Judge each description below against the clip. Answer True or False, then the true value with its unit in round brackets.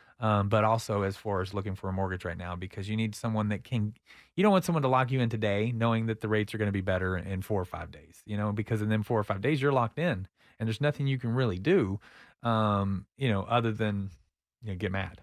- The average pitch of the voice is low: True (105 Hz)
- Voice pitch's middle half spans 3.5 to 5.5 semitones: False (3.1 semitones)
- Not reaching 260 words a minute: False (270 wpm)